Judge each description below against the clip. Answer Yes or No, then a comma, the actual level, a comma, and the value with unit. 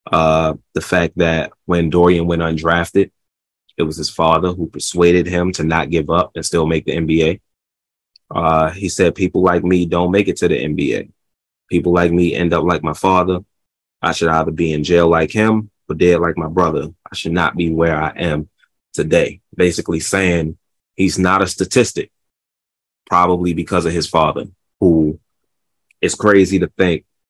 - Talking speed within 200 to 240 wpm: No, average, 180 wpm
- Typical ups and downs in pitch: No, narrow, 2.0 semitones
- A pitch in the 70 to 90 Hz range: Yes, very low, 85 Hz